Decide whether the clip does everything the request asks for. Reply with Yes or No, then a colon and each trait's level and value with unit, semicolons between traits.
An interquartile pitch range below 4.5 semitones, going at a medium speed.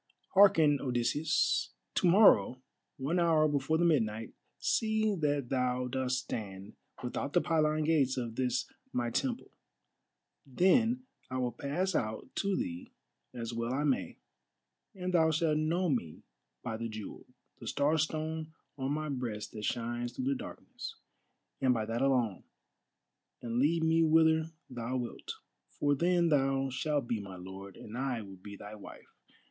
No: average, 5.1 semitones; average, 150 wpm